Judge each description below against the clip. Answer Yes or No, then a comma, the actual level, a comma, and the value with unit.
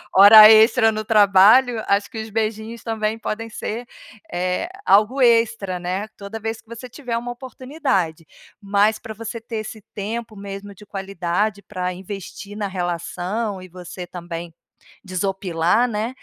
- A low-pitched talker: No, high, 210 Hz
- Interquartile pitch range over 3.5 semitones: No, average, 2.9 semitones